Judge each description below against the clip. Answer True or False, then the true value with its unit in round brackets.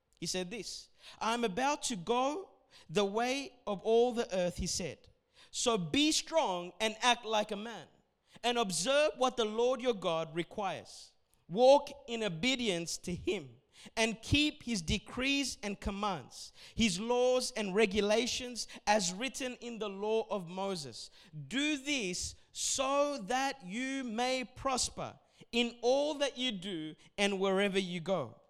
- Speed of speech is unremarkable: True (145 wpm)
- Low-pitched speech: False (230 Hz)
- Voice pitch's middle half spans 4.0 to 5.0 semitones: True (4.6 semitones)